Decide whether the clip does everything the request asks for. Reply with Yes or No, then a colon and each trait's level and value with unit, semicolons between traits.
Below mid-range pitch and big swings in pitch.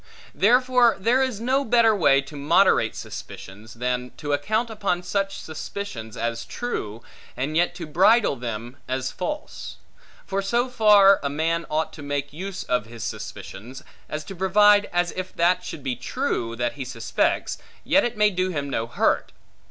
No: medium, 170 Hz; wide, 8.1 semitones